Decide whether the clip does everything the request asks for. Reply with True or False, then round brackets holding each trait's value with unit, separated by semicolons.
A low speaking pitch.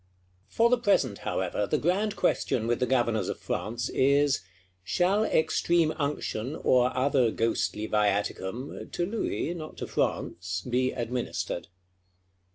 True (130 Hz)